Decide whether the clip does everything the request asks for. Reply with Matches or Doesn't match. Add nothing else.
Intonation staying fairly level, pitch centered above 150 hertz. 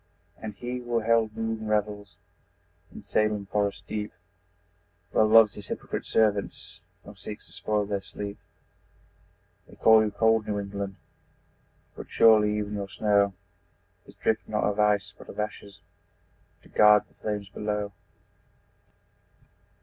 Doesn't match